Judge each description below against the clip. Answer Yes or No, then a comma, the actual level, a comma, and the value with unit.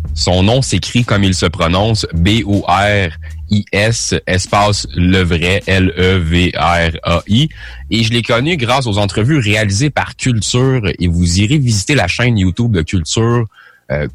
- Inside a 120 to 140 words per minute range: Yes, slow, 135 wpm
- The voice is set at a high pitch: No, low, 100 Hz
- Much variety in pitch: No, average, 4.4 semitones